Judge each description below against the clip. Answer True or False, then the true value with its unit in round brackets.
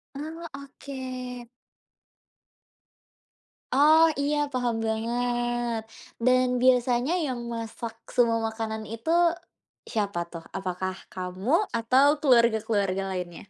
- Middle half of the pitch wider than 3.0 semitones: False (2.7 semitones)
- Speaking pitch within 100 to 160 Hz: False (240 Hz)